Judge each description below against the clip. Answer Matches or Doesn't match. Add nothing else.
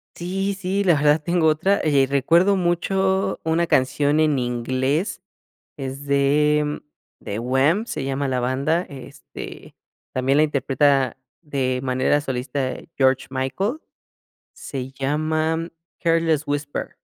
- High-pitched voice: Doesn't match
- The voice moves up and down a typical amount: Matches